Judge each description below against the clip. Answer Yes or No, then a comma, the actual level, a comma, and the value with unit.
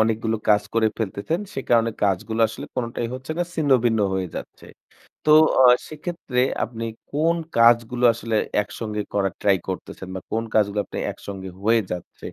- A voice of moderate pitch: No, low, 115 Hz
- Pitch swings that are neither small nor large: Yes, average, 3.1 semitones